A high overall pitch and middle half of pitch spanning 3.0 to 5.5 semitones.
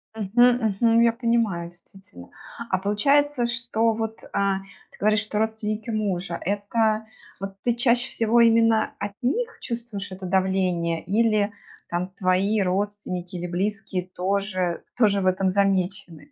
Yes: high, 205 Hz; average, 3.3 semitones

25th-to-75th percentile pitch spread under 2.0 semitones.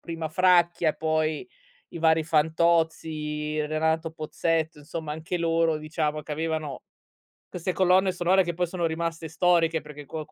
Yes: narrow, 1.5 semitones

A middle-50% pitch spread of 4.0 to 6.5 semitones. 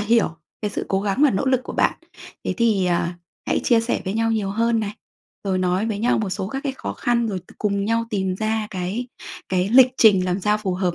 No: average, 3.4 semitones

